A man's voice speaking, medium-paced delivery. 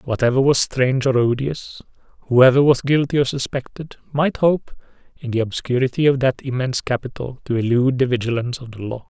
Yes: male; average, 170 wpm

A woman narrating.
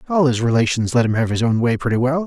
No: male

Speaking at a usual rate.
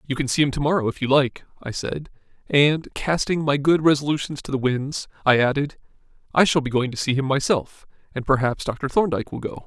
No: fast, 215 wpm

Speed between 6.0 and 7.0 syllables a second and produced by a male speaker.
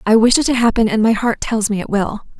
No: 6.2 syllables/s; female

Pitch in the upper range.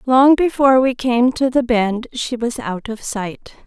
Yes: high, 245 Hz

